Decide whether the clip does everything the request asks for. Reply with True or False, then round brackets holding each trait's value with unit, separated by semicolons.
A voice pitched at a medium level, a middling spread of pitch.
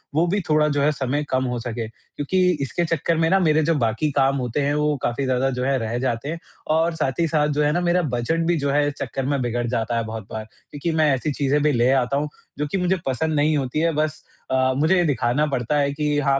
True (145 Hz; 3.3 semitones)